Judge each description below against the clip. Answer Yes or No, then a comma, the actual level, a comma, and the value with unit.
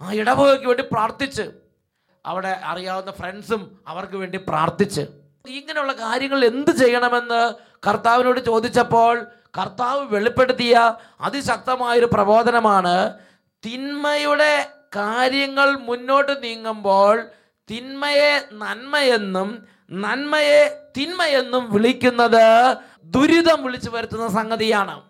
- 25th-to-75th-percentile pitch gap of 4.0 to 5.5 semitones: Yes, average, 4.5 semitones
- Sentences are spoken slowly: Yes, slow, 80 wpm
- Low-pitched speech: No, high, 235 Hz